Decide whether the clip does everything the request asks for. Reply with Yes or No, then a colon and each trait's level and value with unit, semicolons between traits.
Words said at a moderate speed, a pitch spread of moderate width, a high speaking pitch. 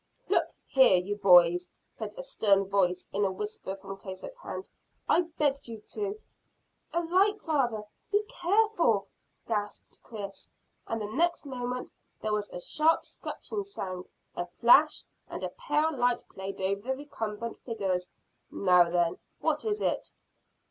No: average, 155 wpm; wide, 8.7 semitones; high, 225 Hz